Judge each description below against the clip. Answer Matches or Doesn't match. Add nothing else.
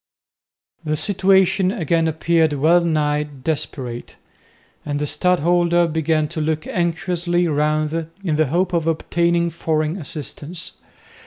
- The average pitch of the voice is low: Doesn't match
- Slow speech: Matches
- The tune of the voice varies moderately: Doesn't match